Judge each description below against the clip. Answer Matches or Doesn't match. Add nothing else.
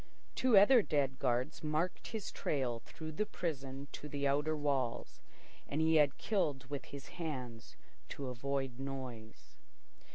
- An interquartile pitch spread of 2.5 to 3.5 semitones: Matches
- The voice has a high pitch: Doesn't match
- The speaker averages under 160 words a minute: Matches